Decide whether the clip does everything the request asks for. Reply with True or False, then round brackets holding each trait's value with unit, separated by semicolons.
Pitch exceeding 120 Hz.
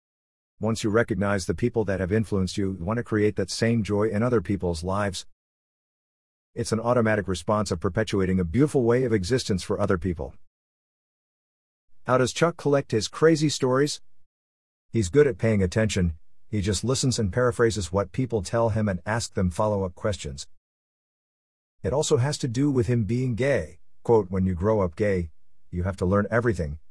False (105 Hz)